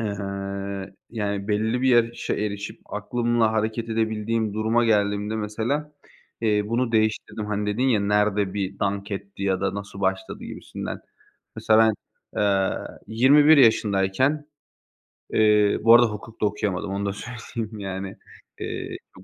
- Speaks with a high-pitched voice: No, low, 105 Hz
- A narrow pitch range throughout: Yes, narrow, 2.2 semitones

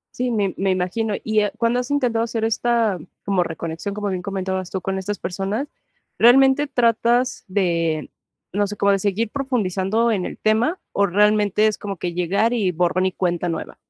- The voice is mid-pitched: No, high, 205 Hz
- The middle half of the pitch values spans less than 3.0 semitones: No, average, 3.7 semitones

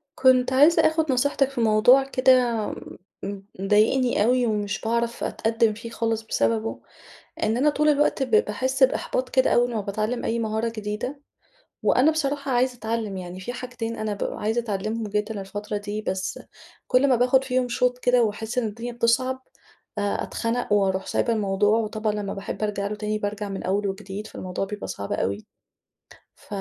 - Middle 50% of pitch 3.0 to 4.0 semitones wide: Yes, average, 3.3 semitones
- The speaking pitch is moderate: No, high, 225 Hz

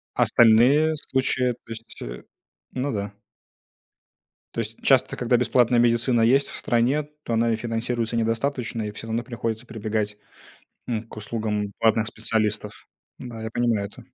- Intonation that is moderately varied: No, narrow, 1.8 semitones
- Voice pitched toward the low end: Yes, low, 115 Hz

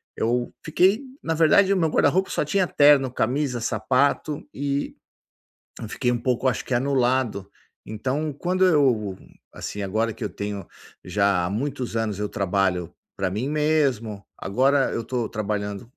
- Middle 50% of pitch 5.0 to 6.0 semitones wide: Yes, wide, 5.4 semitones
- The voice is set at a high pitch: No, low, 125 Hz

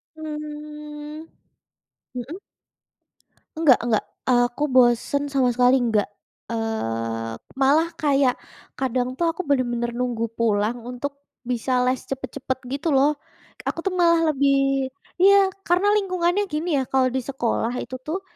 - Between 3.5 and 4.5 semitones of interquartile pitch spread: Yes, average, 3.8 semitones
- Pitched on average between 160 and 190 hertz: No, very high, 270 Hz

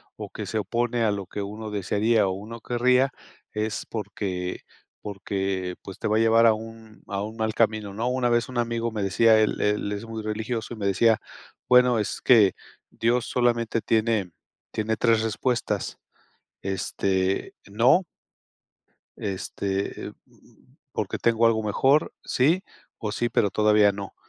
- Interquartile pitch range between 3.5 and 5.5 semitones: No, narrow, 2.4 semitones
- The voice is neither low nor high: No, low, 110 Hz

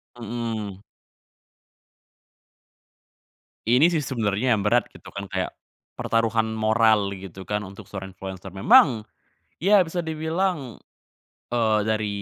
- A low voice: Yes, low, 110 Hz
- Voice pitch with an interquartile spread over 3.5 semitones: Yes, average, 4.0 semitones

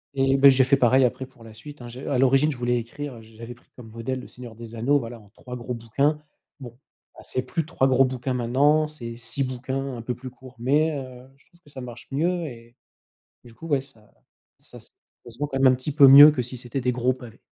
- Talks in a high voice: No, low, 130 Hz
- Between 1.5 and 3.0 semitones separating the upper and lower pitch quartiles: Yes, narrow, 2.5 semitones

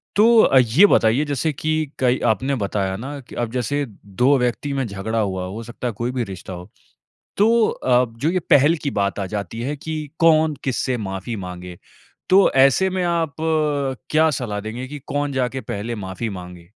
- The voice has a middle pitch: No, low, 125 Hz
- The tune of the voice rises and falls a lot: Yes, wide, 5.7 semitones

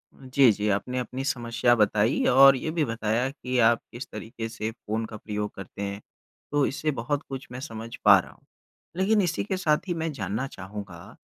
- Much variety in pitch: No, average, 4.3 semitones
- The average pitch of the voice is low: Yes, low, 120 Hz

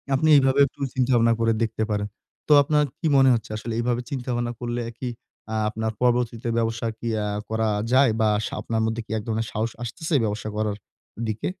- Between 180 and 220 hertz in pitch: No, low, 115 Hz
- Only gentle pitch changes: Yes, narrow, 2.1 semitones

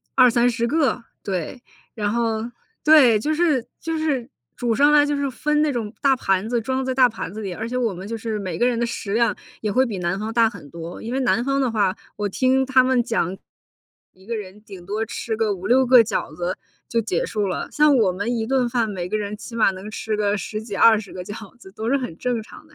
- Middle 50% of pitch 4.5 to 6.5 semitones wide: No, average, 3.8 semitones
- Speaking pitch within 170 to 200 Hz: No, high, 230 Hz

